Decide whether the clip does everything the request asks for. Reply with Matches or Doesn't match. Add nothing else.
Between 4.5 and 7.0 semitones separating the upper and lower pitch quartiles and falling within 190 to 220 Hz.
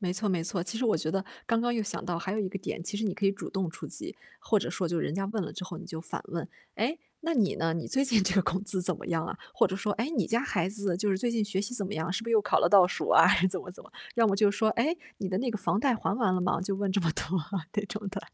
Doesn't match